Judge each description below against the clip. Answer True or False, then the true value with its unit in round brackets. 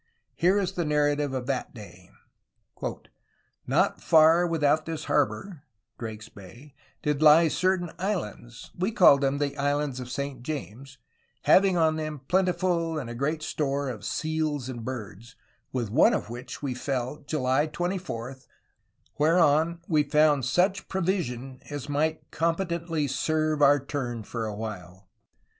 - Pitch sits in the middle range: True (145 Hz)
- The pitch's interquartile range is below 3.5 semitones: False (4.4 semitones)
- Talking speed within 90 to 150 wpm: True (140 wpm)